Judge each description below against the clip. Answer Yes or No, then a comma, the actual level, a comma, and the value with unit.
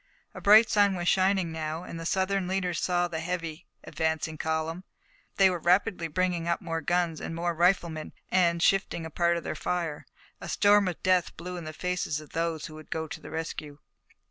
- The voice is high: No, medium, 170 Hz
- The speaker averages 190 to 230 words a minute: Yes, average, 200 wpm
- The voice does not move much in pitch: Yes, narrow, 2.2 semitones